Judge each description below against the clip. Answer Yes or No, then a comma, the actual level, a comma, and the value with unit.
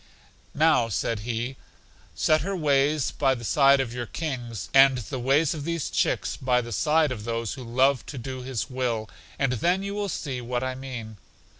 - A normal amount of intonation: Yes, average, 3.5 semitones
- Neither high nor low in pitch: No, low, 130 Hz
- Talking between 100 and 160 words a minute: No, average, 190 wpm